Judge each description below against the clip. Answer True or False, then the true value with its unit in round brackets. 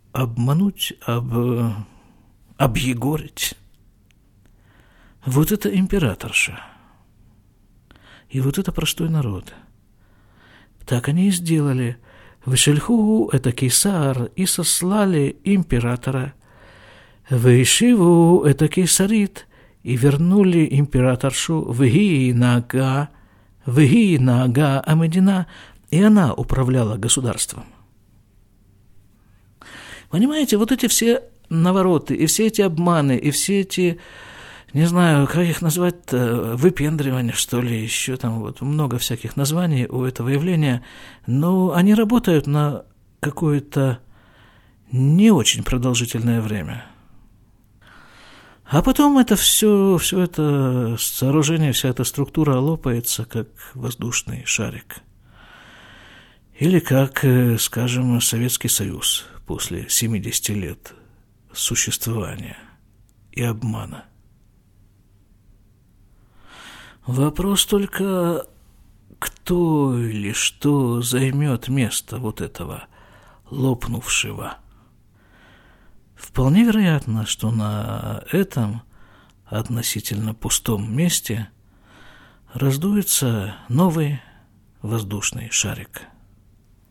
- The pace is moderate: False (85 wpm)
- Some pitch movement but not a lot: False (6.3 semitones)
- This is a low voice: True (125 Hz)